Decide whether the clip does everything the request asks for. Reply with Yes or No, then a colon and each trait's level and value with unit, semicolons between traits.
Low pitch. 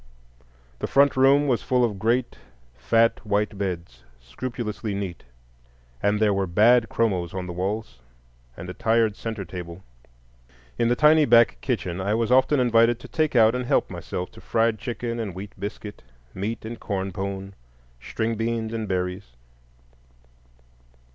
Yes: low, 110 Hz